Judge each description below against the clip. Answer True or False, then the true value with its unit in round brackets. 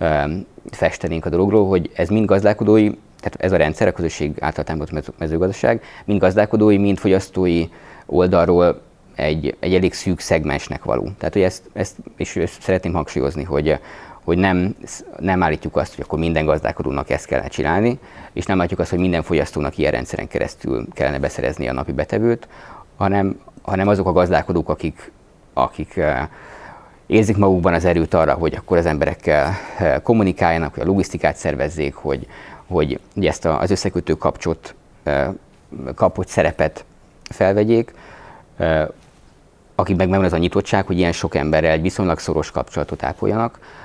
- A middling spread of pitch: True (3.2 semitones)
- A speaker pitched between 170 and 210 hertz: False (90 Hz)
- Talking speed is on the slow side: False (150 wpm)